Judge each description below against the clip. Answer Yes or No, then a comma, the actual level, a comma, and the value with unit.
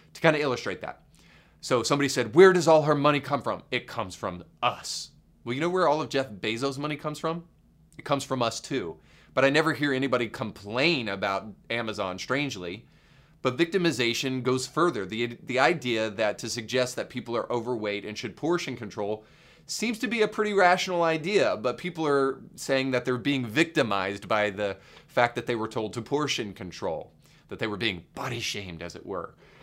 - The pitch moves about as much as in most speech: No, wide, 5.7 semitones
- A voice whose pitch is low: Yes, low, 130 Hz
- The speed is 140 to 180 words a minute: No, average, 195 wpm